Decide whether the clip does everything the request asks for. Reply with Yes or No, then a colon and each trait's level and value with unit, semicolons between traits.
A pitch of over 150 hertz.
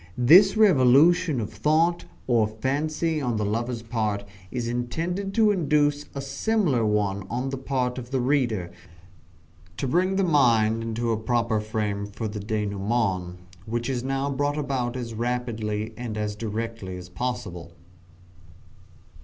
No: low, 120 Hz